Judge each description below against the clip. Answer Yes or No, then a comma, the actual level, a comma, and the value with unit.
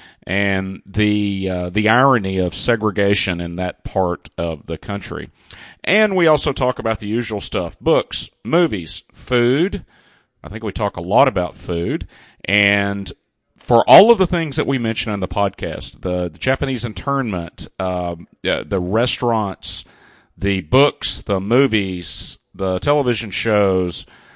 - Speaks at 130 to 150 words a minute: Yes, average, 145 wpm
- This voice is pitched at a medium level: No, low, 100 Hz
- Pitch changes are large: No, average, 4.6 semitones